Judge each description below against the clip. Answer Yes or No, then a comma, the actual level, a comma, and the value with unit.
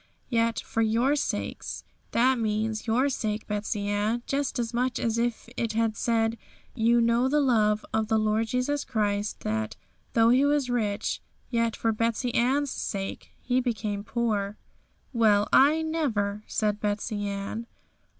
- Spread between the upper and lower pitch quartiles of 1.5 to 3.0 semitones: Yes, narrow, 2.6 semitones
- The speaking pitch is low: No, high, 225 Hz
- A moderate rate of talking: Yes, average, 155 wpm